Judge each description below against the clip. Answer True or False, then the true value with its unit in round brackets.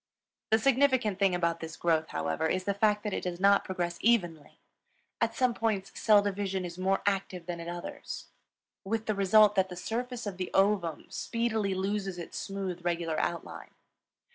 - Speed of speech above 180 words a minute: False (175 wpm)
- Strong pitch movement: False (3.3 semitones)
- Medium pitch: False (195 Hz)